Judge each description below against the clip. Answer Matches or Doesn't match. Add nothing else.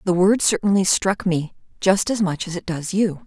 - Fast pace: Matches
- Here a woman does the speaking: Matches